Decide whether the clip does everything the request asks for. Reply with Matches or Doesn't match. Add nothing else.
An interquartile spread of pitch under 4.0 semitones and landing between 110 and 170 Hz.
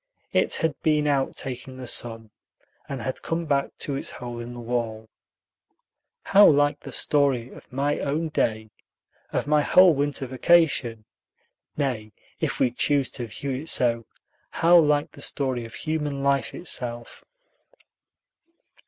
Matches